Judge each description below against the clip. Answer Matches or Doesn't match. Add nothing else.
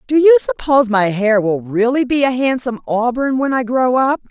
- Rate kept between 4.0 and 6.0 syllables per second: Matches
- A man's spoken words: Doesn't match